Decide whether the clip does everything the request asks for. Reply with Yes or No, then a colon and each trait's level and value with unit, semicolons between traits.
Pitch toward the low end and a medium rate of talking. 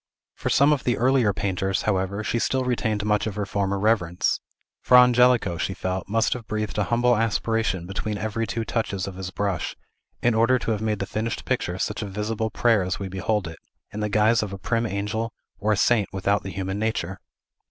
No: low, 105 Hz; fast, 210 wpm